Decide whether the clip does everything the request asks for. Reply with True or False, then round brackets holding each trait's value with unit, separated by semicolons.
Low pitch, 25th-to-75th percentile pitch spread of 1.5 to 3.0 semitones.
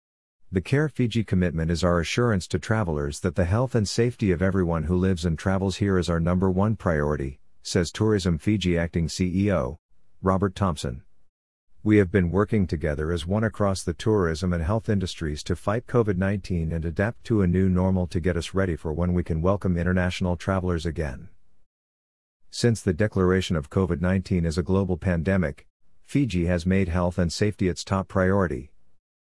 True (90 Hz; 2.7 semitones)